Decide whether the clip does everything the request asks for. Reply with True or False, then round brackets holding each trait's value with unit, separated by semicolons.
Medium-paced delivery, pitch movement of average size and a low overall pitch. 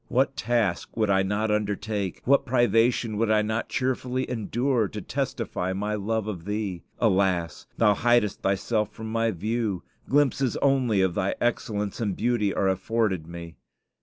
True (155 wpm; 3.4 semitones; 110 Hz)